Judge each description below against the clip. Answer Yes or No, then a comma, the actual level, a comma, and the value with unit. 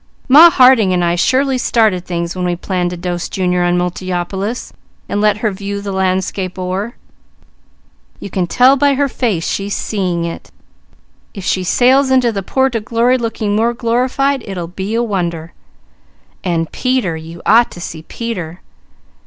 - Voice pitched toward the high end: Yes, high, 200 Hz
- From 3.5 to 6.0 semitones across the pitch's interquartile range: Yes, average, 5.1 semitones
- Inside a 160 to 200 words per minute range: Yes, average, 165 wpm